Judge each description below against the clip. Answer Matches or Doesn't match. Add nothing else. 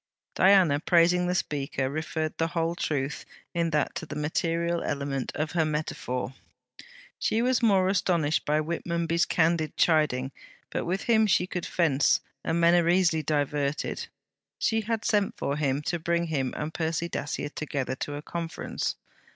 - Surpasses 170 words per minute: Doesn't match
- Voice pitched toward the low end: Doesn't match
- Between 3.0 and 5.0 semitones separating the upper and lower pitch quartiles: Doesn't match